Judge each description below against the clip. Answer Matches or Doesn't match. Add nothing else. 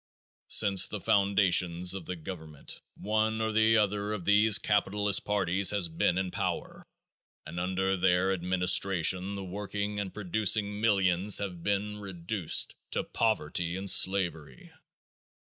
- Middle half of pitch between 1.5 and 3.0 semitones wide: Matches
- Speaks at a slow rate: Matches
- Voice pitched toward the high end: Doesn't match